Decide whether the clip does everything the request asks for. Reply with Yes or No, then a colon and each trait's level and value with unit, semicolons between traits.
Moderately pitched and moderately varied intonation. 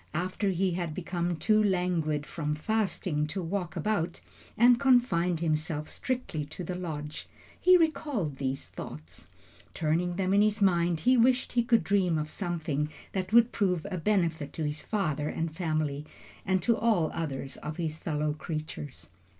Yes: medium, 170 Hz; average, 4.6 semitones